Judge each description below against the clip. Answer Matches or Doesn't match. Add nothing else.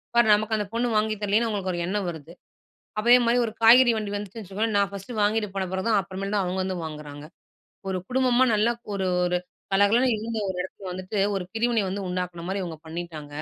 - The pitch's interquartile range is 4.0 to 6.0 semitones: Doesn't match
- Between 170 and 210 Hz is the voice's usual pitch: Matches